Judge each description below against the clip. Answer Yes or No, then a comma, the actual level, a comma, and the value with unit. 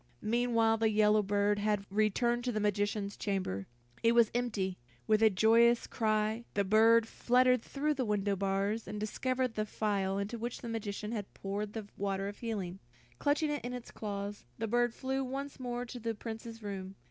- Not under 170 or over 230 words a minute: Yes, average, 180 wpm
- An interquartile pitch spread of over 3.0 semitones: No, average, 2.7 semitones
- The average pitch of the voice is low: No, high, 215 Hz